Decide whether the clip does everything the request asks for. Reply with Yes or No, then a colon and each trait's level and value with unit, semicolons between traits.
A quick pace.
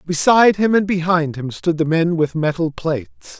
No: average, 195 wpm